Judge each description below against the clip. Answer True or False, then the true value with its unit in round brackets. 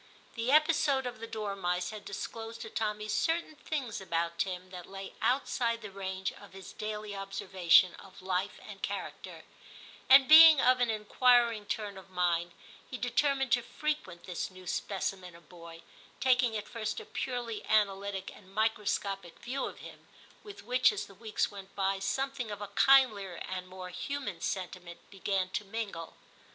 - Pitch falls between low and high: False (205 Hz)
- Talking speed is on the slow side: False (165 wpm)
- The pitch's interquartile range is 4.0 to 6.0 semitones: True (4.3 semitones)